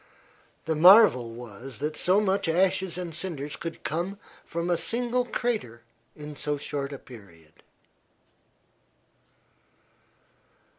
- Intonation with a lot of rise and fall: Yes, wide, 5.9 semitones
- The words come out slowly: Yes, slow, 110 wpm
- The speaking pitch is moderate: Yes, medium, 160 Hz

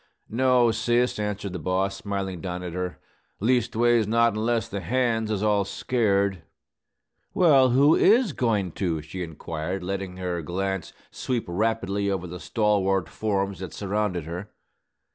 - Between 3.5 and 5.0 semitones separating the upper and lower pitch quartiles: Yes, average, 3.8 semitones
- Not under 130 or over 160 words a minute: Yes, average, 145 wpm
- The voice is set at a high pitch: No, low, 100 Hz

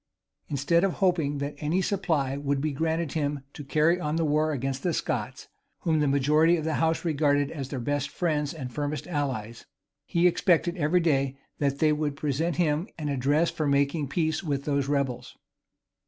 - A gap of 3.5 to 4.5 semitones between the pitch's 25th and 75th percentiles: No, narrow, 2.6 semitones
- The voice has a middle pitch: Yes, medium, 150 Hz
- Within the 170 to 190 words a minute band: Yes, average, 180 wpm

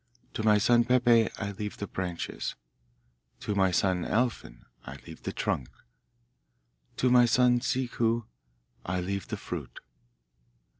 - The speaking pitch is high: No, low, 110 Hz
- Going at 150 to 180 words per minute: No, slow, 135 wpm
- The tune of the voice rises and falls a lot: No, average, 4.4 semitones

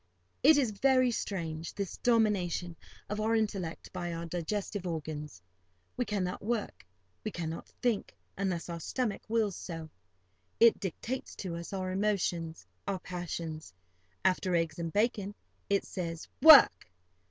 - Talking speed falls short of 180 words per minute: Yes, slow, 135 wpm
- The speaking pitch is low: No, medium, 185 Hz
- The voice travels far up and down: No, average, 4.1 semitones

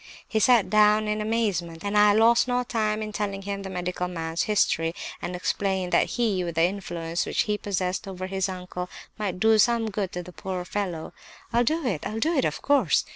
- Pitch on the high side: Yes, high, 200 Hz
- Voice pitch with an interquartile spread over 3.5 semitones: No, average, 3.2 semitones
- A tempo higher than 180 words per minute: Yes, fast, 205 wpm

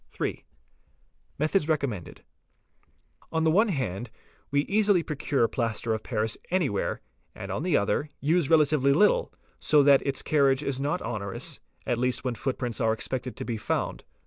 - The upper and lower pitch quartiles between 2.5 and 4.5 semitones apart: No, average, 5.0 semitones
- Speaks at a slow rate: No, average, 165 wpm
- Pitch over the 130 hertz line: Yes, medium, 140 Hz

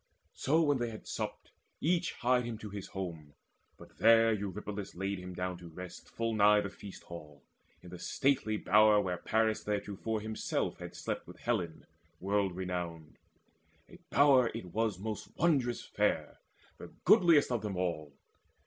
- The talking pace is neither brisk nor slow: Yes, average, 160 wpm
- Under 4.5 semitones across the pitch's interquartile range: Yes, average, 4.0 semitones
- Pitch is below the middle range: Yes, low, 105 Hz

